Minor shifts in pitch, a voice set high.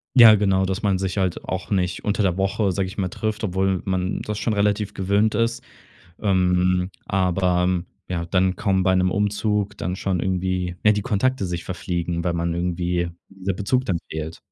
No: narrow, 2.1 semitones; very low, 95 Hz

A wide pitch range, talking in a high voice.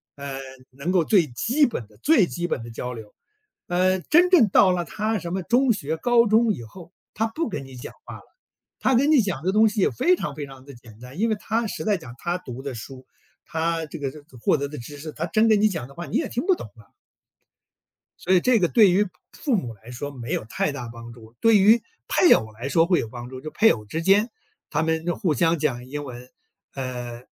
No: wide, 8.5 semitones; medium, 165 Hz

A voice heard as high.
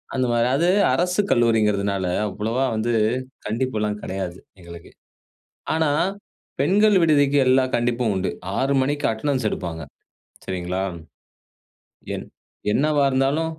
No: low, 120 Hz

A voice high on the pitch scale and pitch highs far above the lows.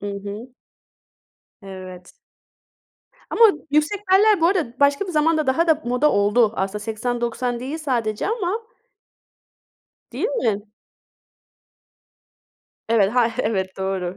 Yes: high, 245 Hz; wide, 7.3 semitones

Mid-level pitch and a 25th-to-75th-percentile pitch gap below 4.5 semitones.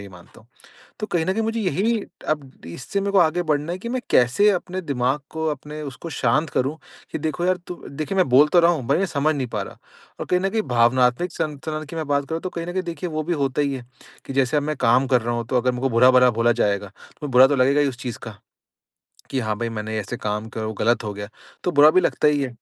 No: medium, 145 Hz; wide, 5.4 semitones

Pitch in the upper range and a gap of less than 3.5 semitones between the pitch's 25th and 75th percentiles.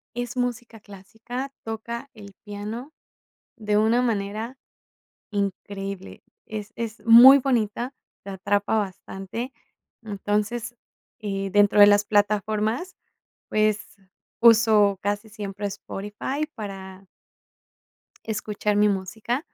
Yes: high, 210 Hz; narrow, 2.5 semitones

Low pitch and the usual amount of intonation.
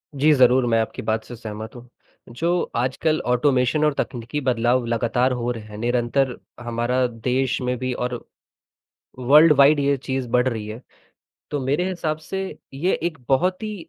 Yes: low, 125 Hz; average, 3.5 semitones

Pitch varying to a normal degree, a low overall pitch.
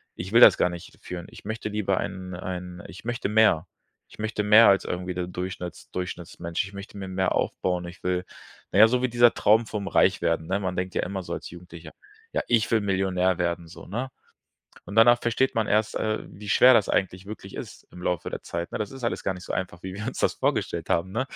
Yes: average, 3.3 semitones; very low, 95 Hz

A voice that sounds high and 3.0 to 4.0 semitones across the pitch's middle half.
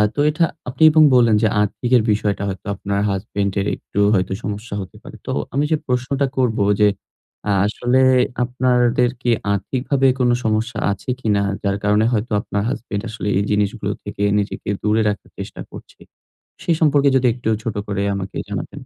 No: low, 110 Hz; average, 3.7 semitones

